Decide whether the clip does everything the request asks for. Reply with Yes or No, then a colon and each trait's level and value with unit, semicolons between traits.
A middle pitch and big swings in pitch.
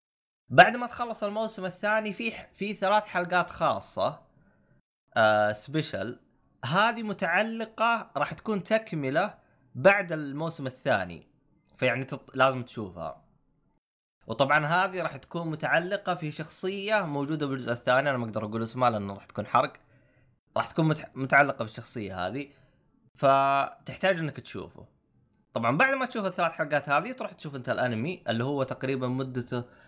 Yes: medium, 145 Hz; wide, 6.9 semitones